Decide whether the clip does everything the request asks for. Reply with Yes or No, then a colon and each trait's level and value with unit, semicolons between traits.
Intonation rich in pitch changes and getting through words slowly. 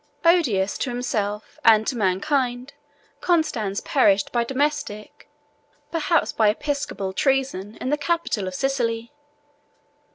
Yes: wide, 5.7 semitones; slow, 110 wpm